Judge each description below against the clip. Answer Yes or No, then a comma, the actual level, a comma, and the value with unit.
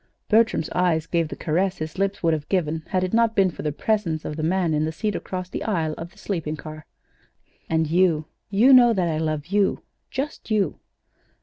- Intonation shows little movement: No, average, 4.1 semitones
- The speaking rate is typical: No, fast, 215 wpm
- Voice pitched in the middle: Yes, medium, 175 Hz